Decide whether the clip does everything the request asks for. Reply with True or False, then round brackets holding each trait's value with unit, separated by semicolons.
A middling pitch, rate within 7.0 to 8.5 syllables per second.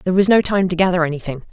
True (175 Hz; 8.0 syllables/s)